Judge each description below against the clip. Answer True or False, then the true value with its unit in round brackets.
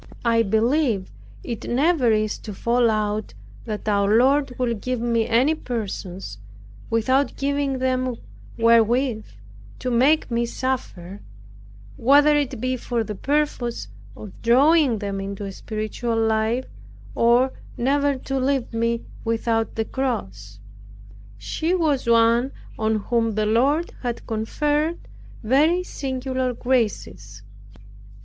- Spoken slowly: True (120 wpm)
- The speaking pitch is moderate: False (235 Hz)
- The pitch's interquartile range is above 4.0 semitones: False (3.4 semitones)